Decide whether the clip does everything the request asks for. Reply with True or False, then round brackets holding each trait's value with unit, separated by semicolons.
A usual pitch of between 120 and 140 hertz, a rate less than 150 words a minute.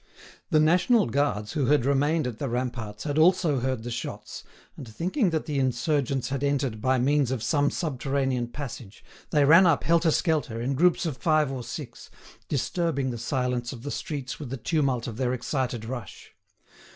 False (135 Hz; 180 wpm)